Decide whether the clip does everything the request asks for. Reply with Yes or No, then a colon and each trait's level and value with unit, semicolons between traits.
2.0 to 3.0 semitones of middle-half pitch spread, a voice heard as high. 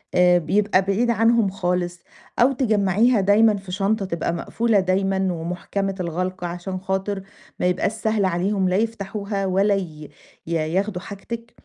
Yes: narrow, 2.6 semitones; high, 195 Hz